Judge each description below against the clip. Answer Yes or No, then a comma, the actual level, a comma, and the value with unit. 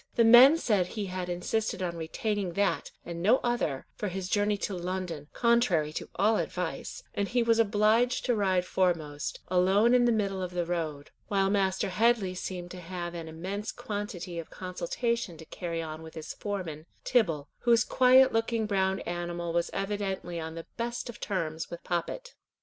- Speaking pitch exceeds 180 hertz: Yes, high, 190 Hz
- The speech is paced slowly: No, average, 180 wpm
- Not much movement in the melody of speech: No, average, 4.1 semitones